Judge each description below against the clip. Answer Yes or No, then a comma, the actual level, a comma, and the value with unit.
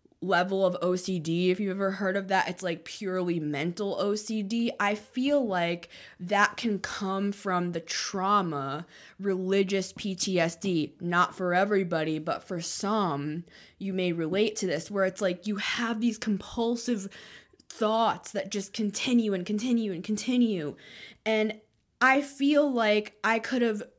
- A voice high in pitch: Yes, high, 195 Hz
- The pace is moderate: Yes, average, 145 wpm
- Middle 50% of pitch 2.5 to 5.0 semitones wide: Yes, average, 3.2 semitones